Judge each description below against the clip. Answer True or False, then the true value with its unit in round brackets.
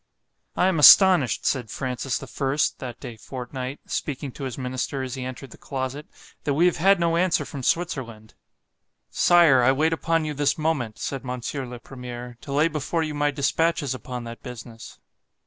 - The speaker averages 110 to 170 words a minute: False (180 wpm)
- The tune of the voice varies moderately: True (3.6 semitones)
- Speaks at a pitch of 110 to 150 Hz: True (135 Hz)